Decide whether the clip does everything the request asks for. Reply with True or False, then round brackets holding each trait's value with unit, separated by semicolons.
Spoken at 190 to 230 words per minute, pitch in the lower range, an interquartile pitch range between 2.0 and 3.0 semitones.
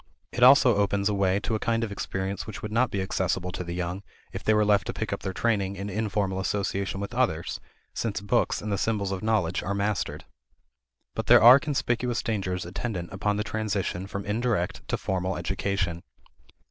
True (200 wpm; 100 Hz; 2.4 semitones)